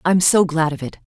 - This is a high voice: No, medium, 165 Hz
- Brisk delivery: Yes, fast, 270 wpm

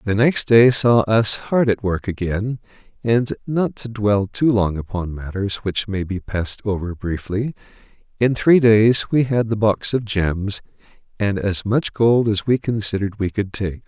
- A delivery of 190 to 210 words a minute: No, average, 180 wpm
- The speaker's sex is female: No, male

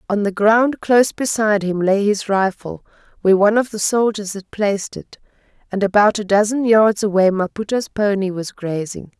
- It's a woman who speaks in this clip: Yes, female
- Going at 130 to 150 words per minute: No, average, 175 wpm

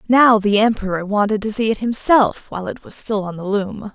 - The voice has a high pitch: Yes, high, 210 Hz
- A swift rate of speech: Yes, fast, 230 wpm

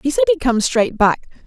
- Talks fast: Yes, fast, 245 wpm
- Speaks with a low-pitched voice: No, high, 240 Hz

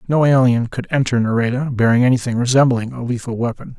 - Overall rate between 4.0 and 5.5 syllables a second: No, 6.4 syllables/s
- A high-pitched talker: No, low, 125 Hz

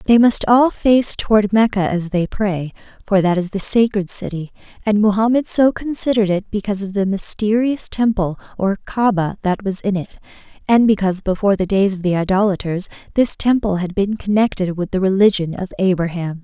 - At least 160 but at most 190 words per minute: Yes, average, 180 wpm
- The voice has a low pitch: No, high, 200 Hz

